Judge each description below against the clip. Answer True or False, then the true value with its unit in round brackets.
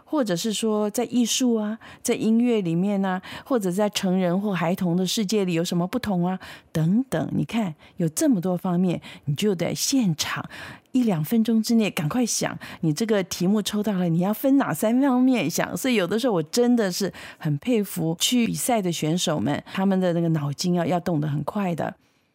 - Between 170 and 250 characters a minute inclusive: False (290 characters per minute)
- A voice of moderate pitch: False (200 Hz)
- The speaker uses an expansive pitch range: False (4.6 semitones)